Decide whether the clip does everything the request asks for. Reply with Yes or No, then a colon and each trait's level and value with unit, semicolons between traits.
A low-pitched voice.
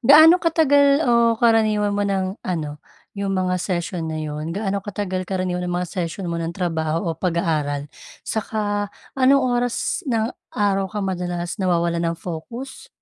No: high, 190 Hz